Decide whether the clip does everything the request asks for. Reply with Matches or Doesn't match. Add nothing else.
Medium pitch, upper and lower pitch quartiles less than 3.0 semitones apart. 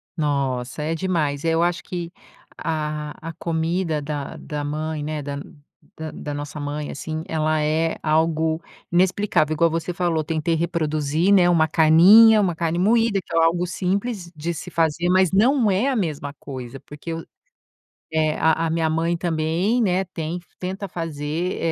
Matches